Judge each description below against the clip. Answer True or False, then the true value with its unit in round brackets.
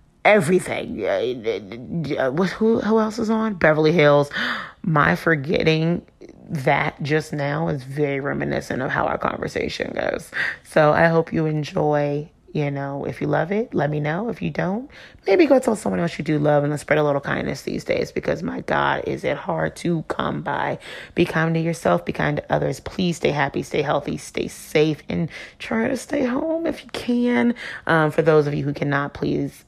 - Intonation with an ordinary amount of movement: False (6.3 semitones)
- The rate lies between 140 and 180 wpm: False (195 wpm)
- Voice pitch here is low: False (160 Hz)